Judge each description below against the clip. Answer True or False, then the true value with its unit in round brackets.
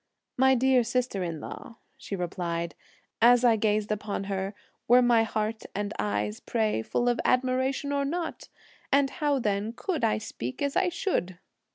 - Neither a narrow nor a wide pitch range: True (5.0 semitones)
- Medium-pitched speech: False (225 Hz)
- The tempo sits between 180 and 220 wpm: False (165 wpm)